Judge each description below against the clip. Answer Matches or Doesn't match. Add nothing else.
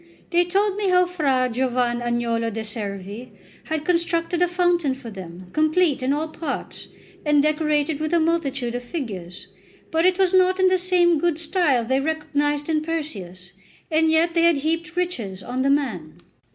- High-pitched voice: Matches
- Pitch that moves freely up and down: Matches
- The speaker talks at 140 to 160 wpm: Doesn't match